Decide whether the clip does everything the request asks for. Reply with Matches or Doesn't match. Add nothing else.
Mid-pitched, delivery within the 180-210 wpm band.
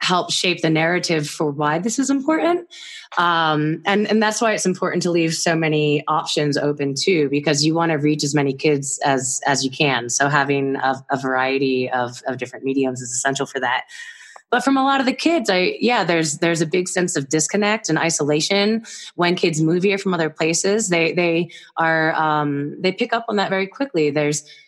Matches